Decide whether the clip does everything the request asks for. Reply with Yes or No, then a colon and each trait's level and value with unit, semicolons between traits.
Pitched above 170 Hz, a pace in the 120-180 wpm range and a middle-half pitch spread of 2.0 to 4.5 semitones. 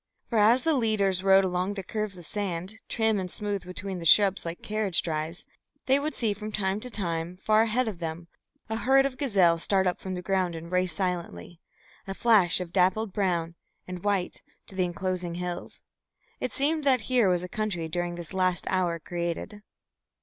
No: high, 190 Hz; average, 195 wpm; average, 3.4 semitones